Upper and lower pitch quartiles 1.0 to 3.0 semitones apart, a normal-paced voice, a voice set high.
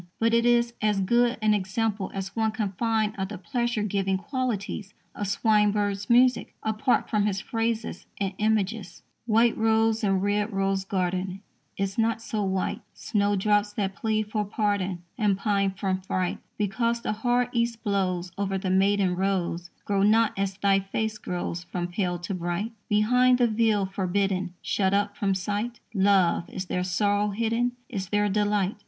Yes: narrow, 2.5 semitones; average, 165 wpm; high, 205 Hz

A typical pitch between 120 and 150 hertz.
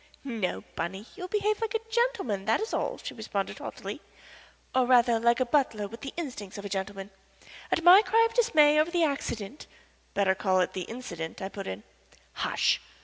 No: high, 240 Hz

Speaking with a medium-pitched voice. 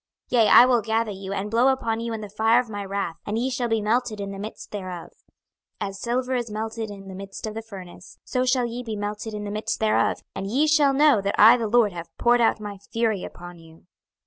No: high, 220 Hz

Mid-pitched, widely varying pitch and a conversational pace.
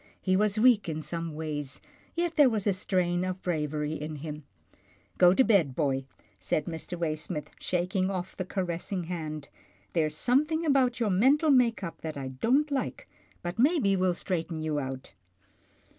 Yes: medium, 180 Hz; wide, 6.0 semitones; average, 175 wpm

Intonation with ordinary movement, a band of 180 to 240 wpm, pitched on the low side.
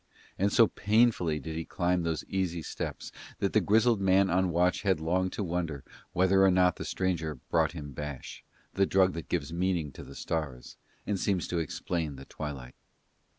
Yes: average, 3.1 semitones; average, 190 wpm; very low, 90 Hz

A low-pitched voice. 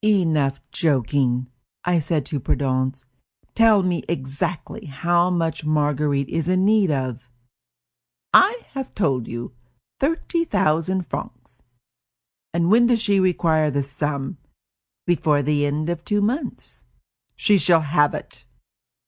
No: medium, 160 Hz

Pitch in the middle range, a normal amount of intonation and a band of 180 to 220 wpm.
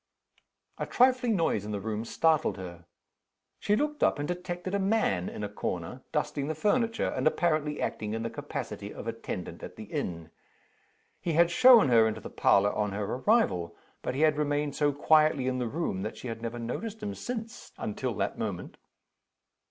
No: medium, 145 Hz; wide, 9.0 semitones; average, 185 wpm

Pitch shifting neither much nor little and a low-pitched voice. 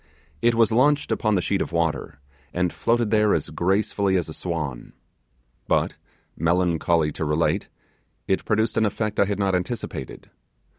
Yes: average, 4.4 semitones; very low, 95 Hz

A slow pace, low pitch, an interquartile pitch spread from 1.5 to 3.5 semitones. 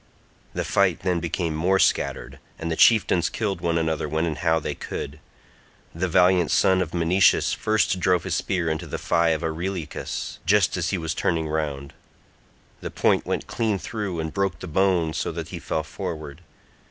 No: average, 180 wpm; very low, 85 Hz; average, 2.8 semitones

